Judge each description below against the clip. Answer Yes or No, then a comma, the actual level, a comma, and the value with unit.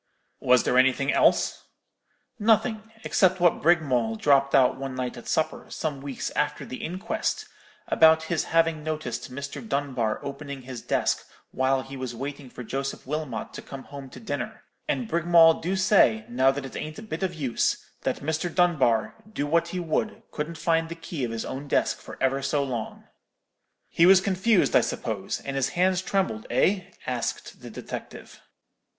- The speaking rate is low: No, average, 175 wpm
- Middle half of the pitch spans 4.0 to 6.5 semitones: Yes, average, 4.6 semitones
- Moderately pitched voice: Yes, medium, 145 Hz